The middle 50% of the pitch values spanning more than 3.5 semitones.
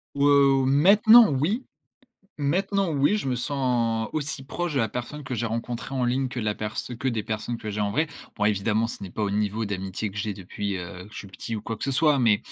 Yes: average, 5.0 semitones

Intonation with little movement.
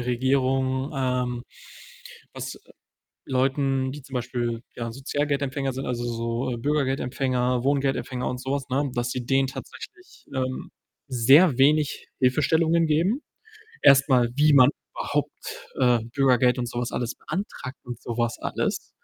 Yes: narrow, 2.0 semitones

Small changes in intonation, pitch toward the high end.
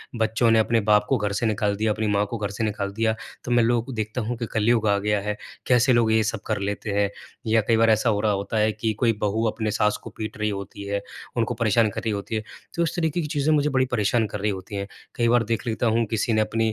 No: narrow, 2.0 semitones; low, 110 Hz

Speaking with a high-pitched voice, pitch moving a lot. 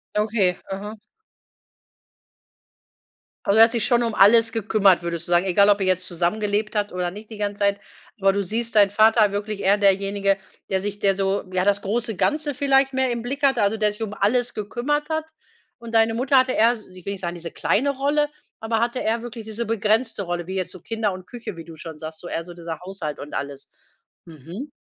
No: high, 205 Hz; average, 3.6 semitones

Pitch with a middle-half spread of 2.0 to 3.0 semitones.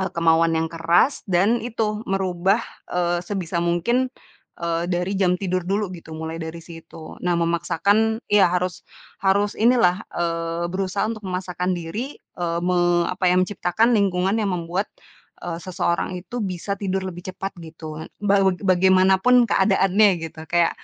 Yes: narrow, 2.6 semitones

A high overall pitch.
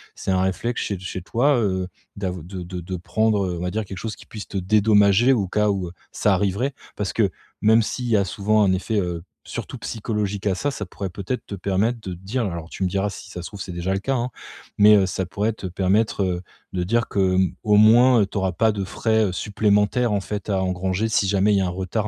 No: low, 100 Hz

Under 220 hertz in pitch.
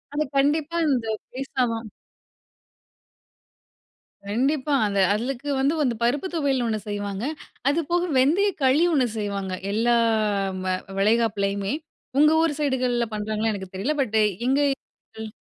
No: high, 245 Hz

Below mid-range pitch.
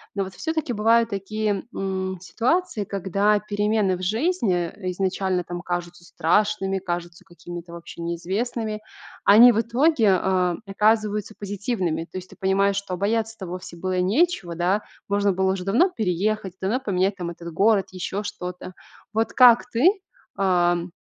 No: high, 195 Hz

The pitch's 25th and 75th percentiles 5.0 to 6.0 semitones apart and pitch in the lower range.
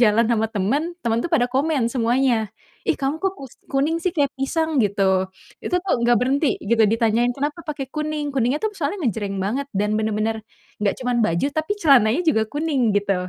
No: average, 5.3 semitones; very high, 250 Hz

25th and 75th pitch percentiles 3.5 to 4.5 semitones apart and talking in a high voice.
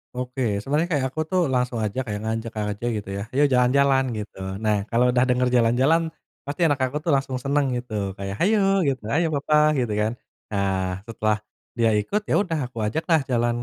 No: average, 4.0 semitones; low, 125 Hz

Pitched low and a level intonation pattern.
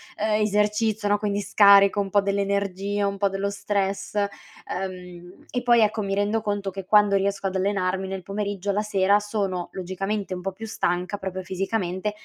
No: high, 200 Hz; narrow, 1.4 semitones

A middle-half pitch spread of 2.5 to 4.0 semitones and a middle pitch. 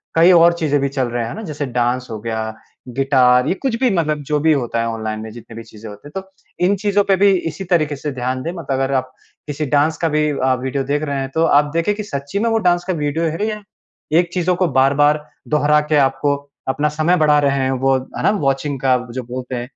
No: average, 4.4 semitones; medium, 145 Hz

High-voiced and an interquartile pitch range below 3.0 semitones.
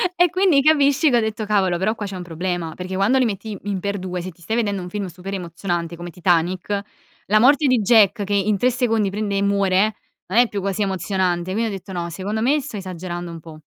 No: high, 195 Hz; average, 3.3 semitones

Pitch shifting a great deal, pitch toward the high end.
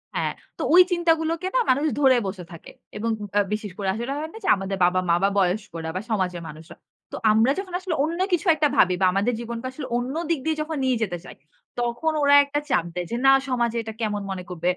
Yes: wide, 7.8 semitones; high, 235 Hz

